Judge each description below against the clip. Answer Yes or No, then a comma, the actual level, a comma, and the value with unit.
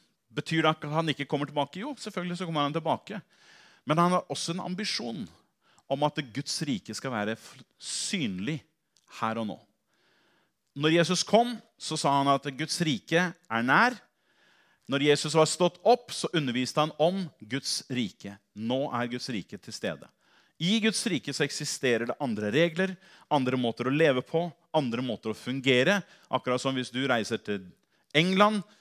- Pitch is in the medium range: Yes, medium, 150 Hz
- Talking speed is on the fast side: No, average, 170 wpm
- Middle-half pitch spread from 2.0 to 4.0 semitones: No, average, 5.2 semitones